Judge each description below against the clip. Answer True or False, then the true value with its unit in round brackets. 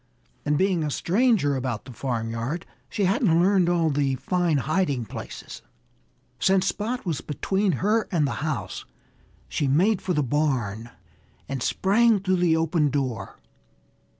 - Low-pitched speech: False (160 Hz)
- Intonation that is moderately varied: False (5.7 semitones)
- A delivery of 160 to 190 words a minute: False (145 wpm)